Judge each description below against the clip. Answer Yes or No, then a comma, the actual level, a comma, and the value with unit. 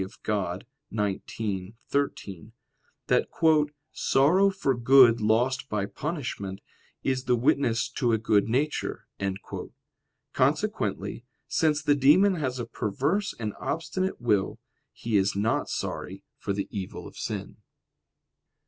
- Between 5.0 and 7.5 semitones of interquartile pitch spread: Yes, wide, 5.6 semitones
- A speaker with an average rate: No, slow, 115 wpm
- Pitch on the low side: Yes, low, 120 Hz